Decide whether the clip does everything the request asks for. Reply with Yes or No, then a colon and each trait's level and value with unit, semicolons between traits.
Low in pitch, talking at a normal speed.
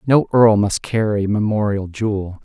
Yes: low, 105 Hz; average, 150 wpm